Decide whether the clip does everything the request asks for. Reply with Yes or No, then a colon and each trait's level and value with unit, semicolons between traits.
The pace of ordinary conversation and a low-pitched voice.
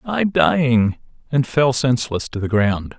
Yes: average, 160 wpm; low, 125 Hz